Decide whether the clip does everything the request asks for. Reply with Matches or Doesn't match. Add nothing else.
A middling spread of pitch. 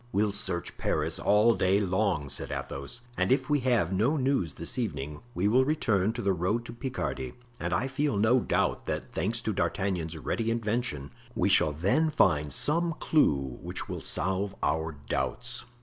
Doesn't match